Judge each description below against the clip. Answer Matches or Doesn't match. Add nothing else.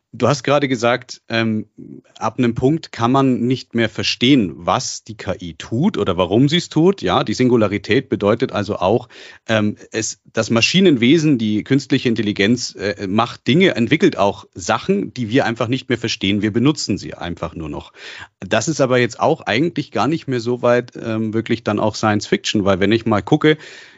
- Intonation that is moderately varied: Matches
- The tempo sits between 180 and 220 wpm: Matches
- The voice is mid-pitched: Doesn't match